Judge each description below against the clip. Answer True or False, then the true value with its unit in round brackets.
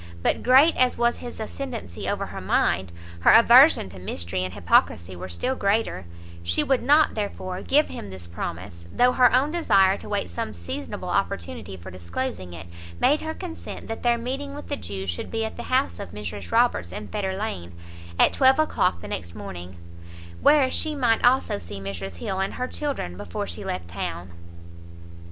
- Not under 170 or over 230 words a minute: True (185 wpm)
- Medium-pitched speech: True (155 Hz)